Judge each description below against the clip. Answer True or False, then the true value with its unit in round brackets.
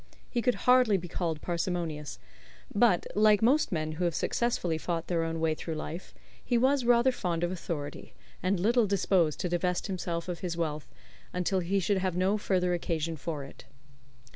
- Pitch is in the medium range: True (180 Hz)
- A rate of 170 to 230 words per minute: True (180 wpm)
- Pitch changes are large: False (3.6 semitones)